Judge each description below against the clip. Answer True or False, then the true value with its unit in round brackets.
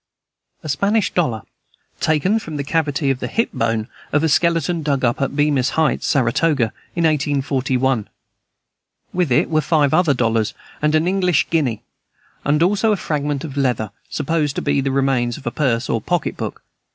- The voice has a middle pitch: True (145 Hz)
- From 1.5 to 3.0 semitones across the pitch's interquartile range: False (3.7 semitones)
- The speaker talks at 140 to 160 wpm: False (175 wpm)